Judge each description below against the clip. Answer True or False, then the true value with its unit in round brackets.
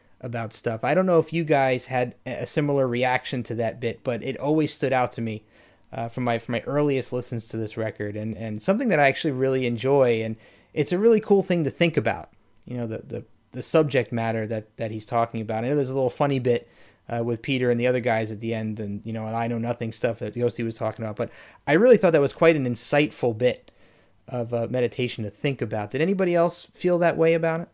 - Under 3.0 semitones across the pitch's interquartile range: False (4.0 semitones)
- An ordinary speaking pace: False (245 wpm)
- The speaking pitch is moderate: False (120 Hz)